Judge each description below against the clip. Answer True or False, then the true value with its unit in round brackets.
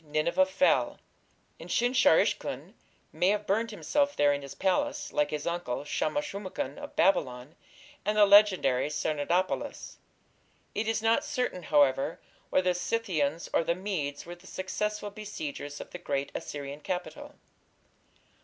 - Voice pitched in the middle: True (180 Hz)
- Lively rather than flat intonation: True (6.2 semitones)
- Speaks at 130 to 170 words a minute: True (150 wpm)